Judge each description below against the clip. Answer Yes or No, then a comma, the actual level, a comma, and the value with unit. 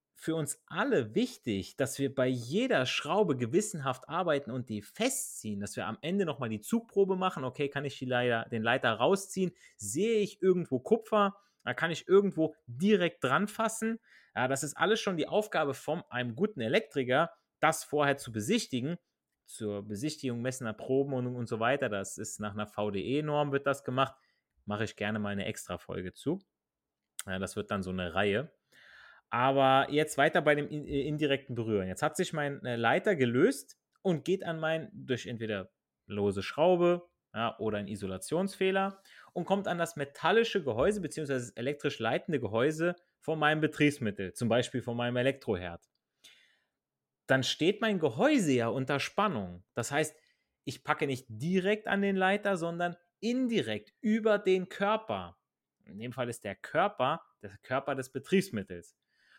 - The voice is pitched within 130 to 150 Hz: Yes, medium, 140 Hz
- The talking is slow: No, average, 160 wpm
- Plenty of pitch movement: Yes, wide, 7.3 semitones